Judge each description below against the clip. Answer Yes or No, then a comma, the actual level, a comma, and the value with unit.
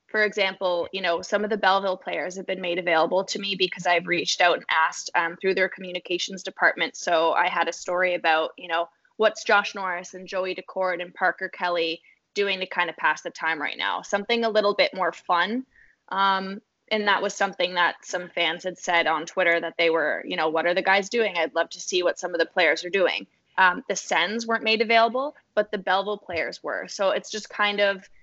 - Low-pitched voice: No, medium, 185 Hz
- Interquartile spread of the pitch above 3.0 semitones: No, narrow, 2.6 semitones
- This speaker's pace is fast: Yes, fast, 225 wpm